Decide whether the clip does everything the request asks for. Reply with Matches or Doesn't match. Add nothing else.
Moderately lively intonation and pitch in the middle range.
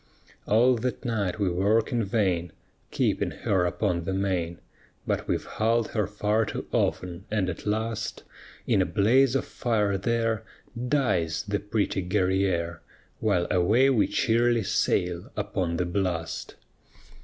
Doesn't match